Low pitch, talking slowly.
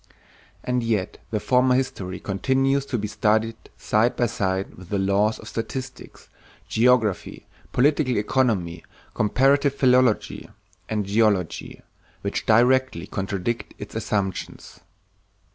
Yes: low, 110 Hz; slow, 110 wpm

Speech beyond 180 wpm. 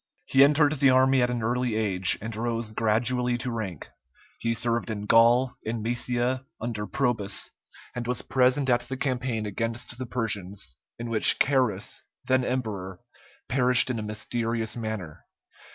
No: average, 150 wpm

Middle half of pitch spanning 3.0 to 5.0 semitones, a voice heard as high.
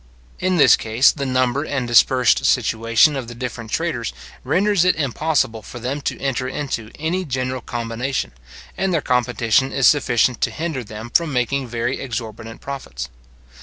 No: average, 3.6 semitones; low, 130 Hz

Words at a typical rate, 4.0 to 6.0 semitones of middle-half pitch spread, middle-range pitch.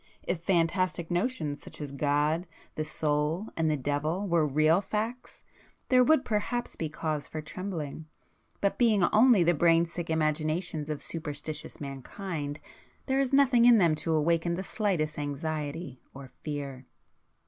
Yes: average, 145 wpm; average, 4.3 semitones; medium, 160 Hz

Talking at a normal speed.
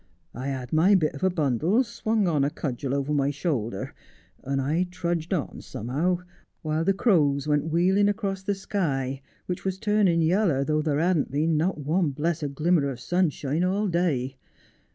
Yes: average, 175 wpm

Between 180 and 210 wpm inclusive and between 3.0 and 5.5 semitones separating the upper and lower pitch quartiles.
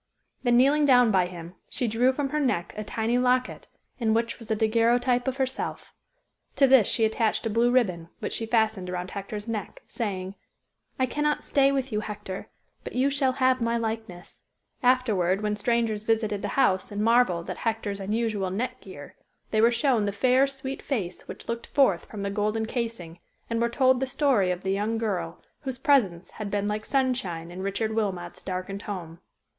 Yes: average, 190 wpm; average, 4.1 semitones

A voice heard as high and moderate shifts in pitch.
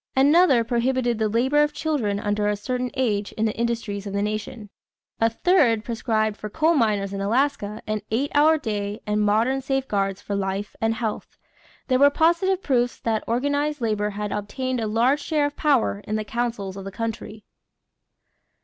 Yes: high, 230 Hz; average, 4.3 semitones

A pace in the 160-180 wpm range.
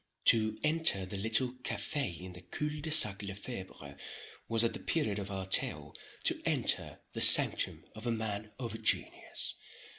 Yes: average, 170 wpm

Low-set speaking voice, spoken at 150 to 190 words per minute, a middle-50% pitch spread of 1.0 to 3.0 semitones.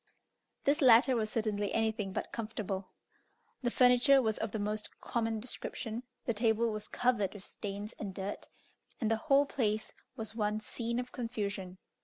No: high, 220 Hz; average, 160 wpm; narrow, 2.5 semitones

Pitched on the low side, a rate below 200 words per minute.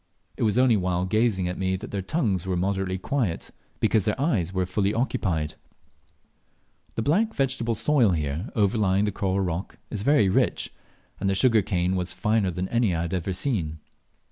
Yes: very low, 95 Hz; average, 180 wpm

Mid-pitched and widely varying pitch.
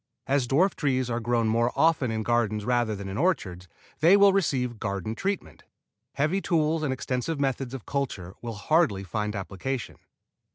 No: low, 125 Hz; wide, 5.8 semitones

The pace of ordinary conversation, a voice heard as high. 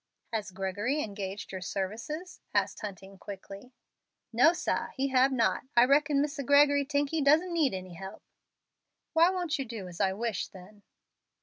Yes: average, 165 wpm; high, 240 Hz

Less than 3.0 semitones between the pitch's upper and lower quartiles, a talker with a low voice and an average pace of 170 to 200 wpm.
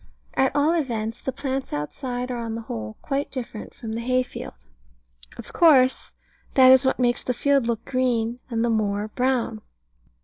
No: narrow, 2.6 semitones; high, 245 Hz; average, 175 wpm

